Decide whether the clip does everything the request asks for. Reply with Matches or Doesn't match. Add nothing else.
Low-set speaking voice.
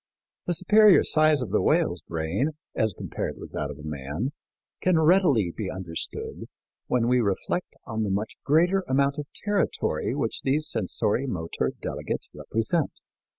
Matches